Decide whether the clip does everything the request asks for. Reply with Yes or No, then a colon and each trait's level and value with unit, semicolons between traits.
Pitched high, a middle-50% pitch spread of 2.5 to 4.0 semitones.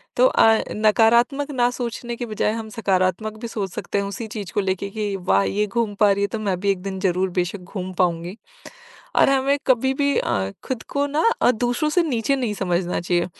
No: high, 210 Hz; average, 4.4 semitones